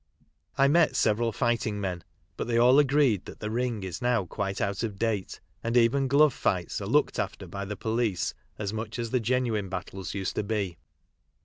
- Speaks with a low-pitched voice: Yes, low, 110 Hz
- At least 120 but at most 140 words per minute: No, average, 165 wpm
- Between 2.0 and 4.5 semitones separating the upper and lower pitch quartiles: Yes, average, 3.7 semitones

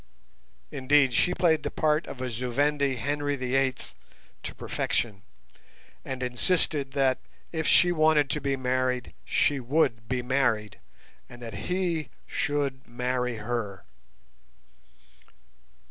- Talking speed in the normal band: No, slow, 125 wpm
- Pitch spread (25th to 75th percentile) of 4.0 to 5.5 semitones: No, average, 3.0 semitones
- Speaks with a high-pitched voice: No, low, 130 Hz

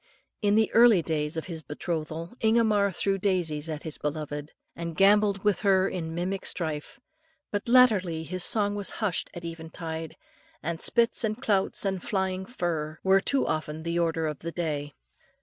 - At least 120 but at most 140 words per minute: No, average, 165 wpm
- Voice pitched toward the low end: No, medium, 175 Hz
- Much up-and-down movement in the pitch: No, average, 4.0 semitones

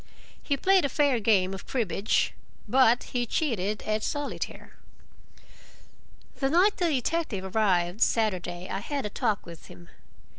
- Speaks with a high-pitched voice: Yes, high, 225 Hz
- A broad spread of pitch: Yes, wide, 6.6 semitones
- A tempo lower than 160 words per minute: Yes, average, 140 wpm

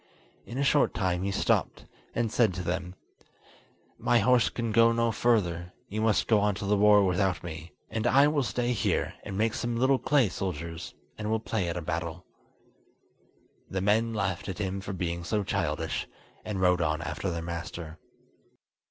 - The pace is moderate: Yes, average, 180 wpm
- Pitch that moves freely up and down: No, average, 4.6 semitones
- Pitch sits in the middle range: No, low, 100 Hz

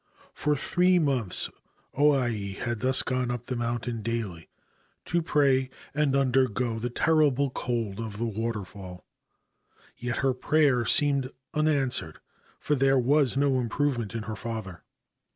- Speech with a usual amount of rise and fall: Yes, average, 3.5 semitones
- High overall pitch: No, low, 125 Hz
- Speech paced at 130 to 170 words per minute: Yes, average, 140 wpm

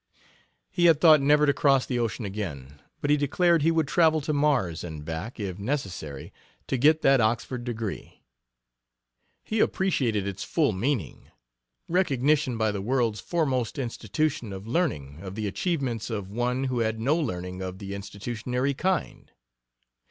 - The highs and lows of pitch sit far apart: Yes, wide, 6.7 semitones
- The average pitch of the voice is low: Yes, low, 120 Hz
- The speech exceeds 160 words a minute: No, average, 155 wpm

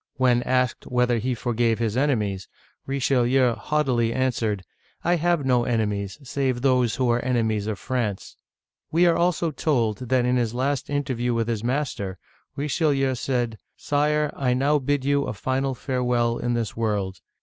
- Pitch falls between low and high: No, low, 125 Hz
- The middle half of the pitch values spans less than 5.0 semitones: Yes, average, 3.0 semitones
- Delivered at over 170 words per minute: No, average, 165 wpm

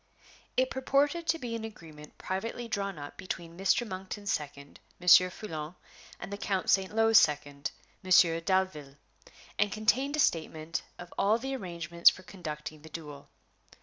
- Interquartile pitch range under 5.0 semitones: No, wide, 5.5 semitones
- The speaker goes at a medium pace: Yes, average, 150 wpm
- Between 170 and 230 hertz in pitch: Yes, medium, 185 Hz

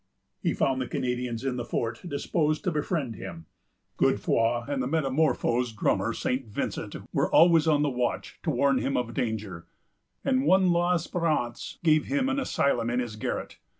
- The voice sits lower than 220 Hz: Yes, low, 135 Hz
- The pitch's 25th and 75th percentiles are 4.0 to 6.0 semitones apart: Yes, average, 4.7 semitones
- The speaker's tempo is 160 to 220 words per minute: Yes, average, 165 wpm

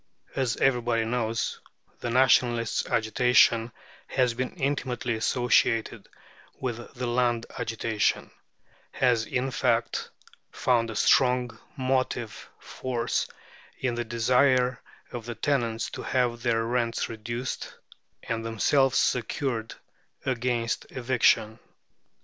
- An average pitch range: No, narrow, 1.8 semitones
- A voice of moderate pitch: No, low, 120 Hz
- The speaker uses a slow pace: Yes, slow, 105 wpm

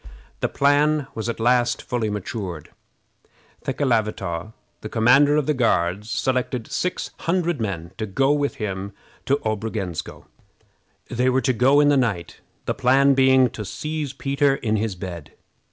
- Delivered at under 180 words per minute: Yes, average, 150 wpm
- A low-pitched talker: Yes, low, 125 Hz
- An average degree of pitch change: Yes, average, 4.7 semitones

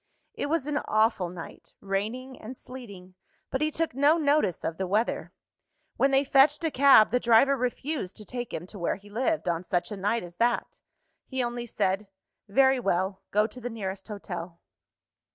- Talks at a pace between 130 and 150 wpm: No, average, 185 wpm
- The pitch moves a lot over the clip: Yes, wide, 5.7 semitones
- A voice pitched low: No, high, 230 Hz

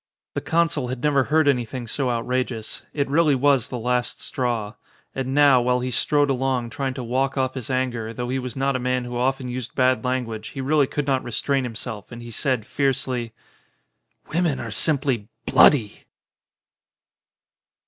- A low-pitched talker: Yes, low, 130 Hz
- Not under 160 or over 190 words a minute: Yes, average, 175 wpm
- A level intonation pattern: Yes, narrow, 2.1 semitones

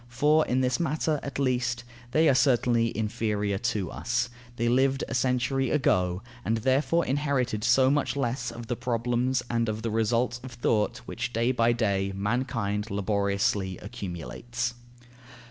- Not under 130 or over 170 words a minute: Yes, average, 155 wpm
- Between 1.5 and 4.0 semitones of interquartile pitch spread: Yes, average, 3.2 semitones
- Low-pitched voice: Yes, low, 120 Hz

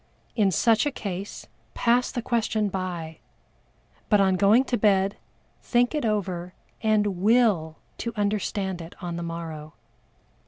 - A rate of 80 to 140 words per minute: Yes, slow, 135 wpm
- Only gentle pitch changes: No, average, 3.9 semitones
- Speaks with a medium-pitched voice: No, high, 200 Hz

